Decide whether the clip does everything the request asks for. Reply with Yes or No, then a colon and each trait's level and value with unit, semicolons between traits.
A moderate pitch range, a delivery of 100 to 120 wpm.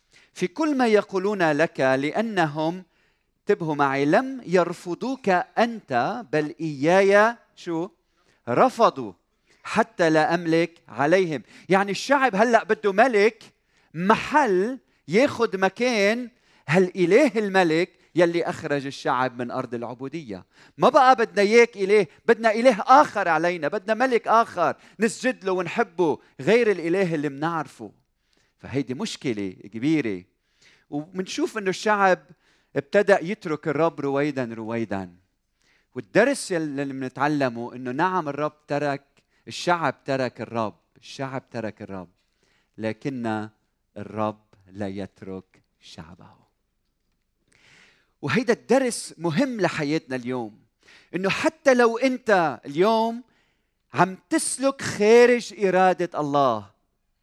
No: wide, 7.8 semitones; average, 105 wpm